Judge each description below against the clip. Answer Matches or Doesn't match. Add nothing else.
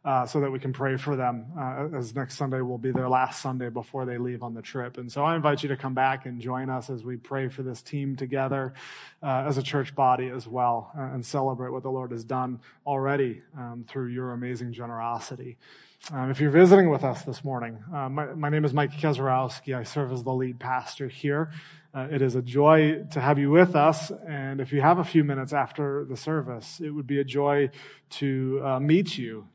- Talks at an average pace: Doesn't match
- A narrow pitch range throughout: Matches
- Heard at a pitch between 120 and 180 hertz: Matches